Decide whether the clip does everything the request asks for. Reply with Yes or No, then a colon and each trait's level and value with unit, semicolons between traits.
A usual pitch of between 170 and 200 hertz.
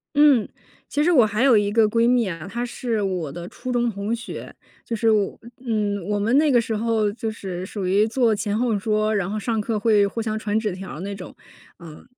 No: high, 215 Hz